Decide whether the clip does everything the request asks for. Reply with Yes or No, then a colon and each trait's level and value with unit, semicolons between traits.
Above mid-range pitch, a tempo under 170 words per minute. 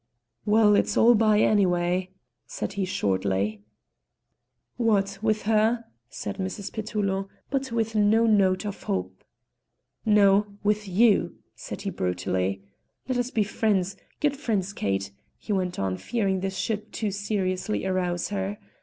Yes: high, 200 Hz; slow, 135 wpm